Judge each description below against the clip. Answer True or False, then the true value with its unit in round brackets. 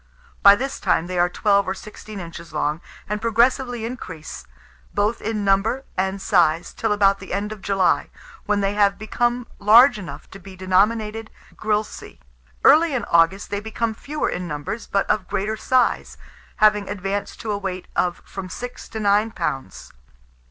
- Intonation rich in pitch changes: False (2.7 semitones)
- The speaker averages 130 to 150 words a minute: False (165 wpm)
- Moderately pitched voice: False (205 Hz)